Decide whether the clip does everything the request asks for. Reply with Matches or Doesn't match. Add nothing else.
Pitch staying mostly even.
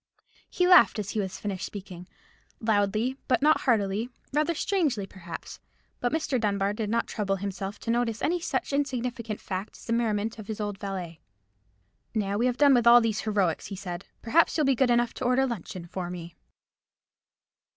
Doesn't match